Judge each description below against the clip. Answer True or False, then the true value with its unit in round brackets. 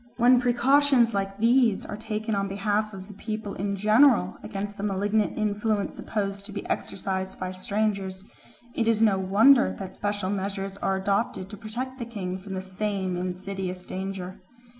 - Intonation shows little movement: True (2.3 semitones)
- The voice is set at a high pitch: True (205 Hz)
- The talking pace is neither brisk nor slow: True (165 wpm)